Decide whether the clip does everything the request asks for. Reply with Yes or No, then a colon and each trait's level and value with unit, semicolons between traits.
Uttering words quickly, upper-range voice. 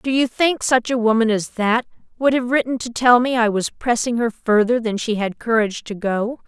Yes: fast, 230 wpm; high, 235 Hz